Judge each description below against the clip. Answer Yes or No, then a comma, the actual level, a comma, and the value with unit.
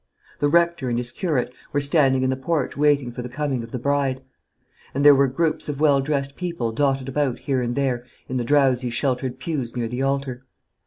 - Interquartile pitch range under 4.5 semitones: Yes, narrow, 2.5 semitones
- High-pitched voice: No, low, 135 Hz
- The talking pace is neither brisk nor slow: No, fast, 210 wpm